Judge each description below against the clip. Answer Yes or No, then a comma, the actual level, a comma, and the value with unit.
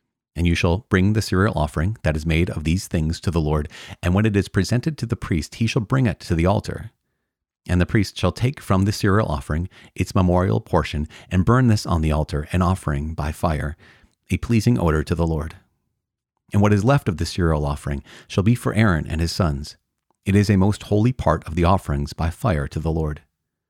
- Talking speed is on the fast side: Yes, fast, 225 wpm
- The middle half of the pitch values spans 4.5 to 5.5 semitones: Yes, average, 4.8 semitones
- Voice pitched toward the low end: Yes, very low, 90 Hz